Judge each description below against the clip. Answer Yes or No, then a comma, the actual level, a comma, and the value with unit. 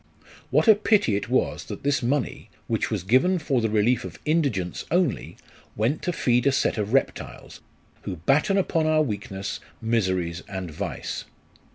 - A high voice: No, low, 125 Hz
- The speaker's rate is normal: Yes, average, 165 wpm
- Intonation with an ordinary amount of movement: No, wide, 7.2 semitones